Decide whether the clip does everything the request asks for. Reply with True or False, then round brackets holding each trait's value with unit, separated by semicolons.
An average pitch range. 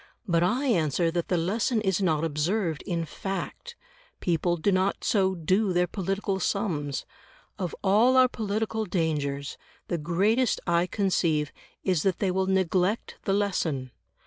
True (3.5 semitones)